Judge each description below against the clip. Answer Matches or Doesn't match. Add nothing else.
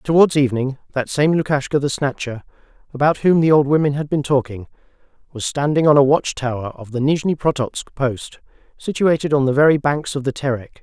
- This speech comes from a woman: Doesn't match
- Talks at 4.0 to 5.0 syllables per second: Doesn't match